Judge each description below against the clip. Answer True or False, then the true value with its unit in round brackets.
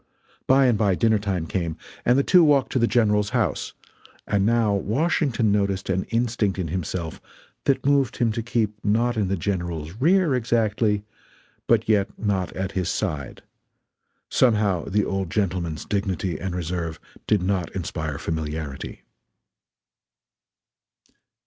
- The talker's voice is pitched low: True (100 Hz)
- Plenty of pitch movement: False (4.2 semitones)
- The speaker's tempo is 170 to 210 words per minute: False (140 wpm)